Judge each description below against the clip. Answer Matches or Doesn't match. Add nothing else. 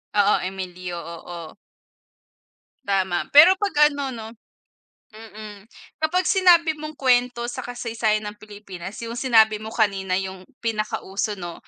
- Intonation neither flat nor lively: Matches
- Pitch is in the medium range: Doesn't match